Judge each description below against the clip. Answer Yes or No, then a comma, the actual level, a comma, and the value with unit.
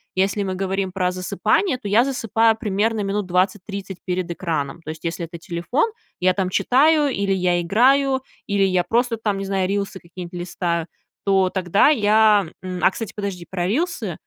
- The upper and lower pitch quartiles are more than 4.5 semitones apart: No, average, 3.4 semitones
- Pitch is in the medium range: No, high, 195 Hz